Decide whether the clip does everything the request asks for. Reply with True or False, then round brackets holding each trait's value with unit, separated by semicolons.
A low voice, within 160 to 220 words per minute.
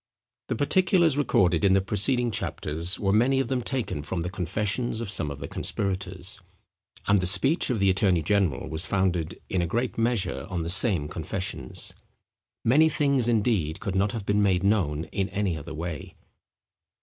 True (100 Hz; 175 wpm)